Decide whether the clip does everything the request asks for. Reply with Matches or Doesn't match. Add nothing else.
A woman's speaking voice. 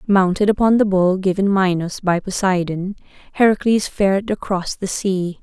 Matches